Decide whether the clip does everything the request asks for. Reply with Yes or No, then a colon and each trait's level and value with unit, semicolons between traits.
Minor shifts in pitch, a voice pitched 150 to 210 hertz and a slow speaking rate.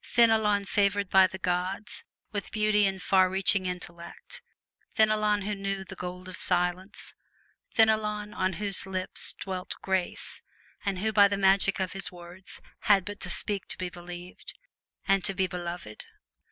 No: narrow, 2.1 semitones; high, 190 Hz; average, 155 wpm